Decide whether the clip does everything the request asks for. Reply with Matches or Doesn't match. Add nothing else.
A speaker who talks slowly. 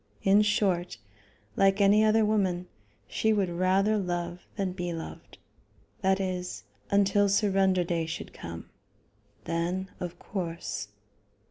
Matches